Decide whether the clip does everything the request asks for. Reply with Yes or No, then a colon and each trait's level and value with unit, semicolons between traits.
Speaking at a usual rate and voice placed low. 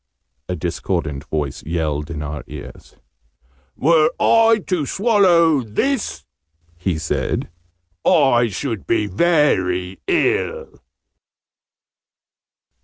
No: slow, 90 wpm; low, 115 Hz